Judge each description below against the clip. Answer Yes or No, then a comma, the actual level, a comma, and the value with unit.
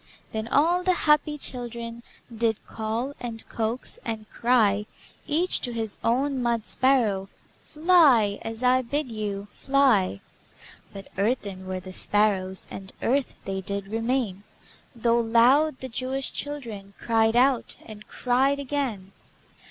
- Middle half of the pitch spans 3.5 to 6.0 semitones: Yes, average, 4.1 semitones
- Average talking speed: No, slow, 130 wpm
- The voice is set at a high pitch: Yes, high, 230 Hz